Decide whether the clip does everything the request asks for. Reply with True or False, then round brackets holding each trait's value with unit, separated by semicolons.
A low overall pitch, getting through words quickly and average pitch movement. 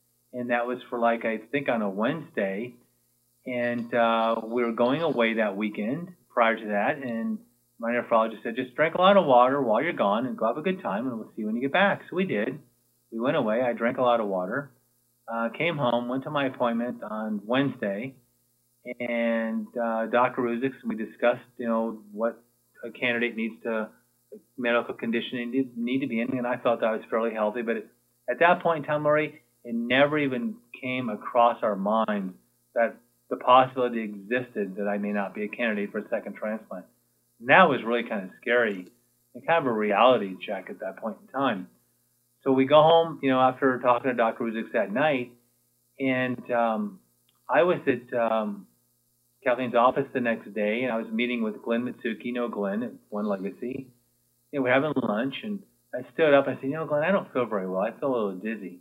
True (120 Hz; 210 wpm; 3.1 semitones)